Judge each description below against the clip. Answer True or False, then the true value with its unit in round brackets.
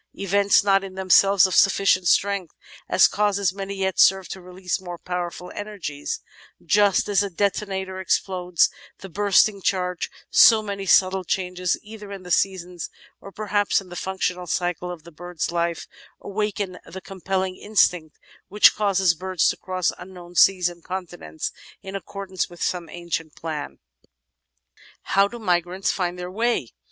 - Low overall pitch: False (185 Hz)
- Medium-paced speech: True (150 wpm)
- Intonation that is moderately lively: False (1.9 semitones)